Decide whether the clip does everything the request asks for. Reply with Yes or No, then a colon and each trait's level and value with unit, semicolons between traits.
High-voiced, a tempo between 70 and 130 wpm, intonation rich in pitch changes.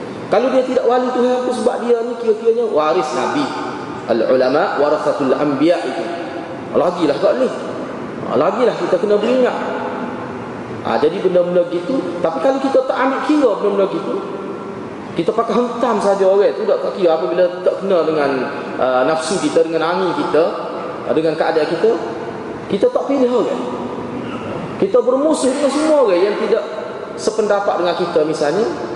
No: high, 245 Hz; average, 145 wpm; wide, 6.2 semitones